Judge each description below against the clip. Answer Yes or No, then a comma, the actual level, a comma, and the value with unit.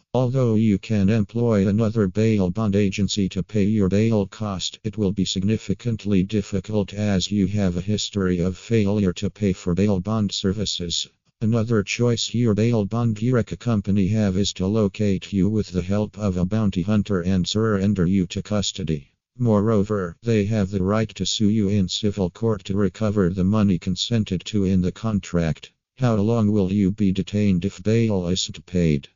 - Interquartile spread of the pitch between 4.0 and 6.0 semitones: No, narrow, 2.5 semitones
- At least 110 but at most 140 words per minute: No, average, 175 wpm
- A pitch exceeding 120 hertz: No, low, 100 Hz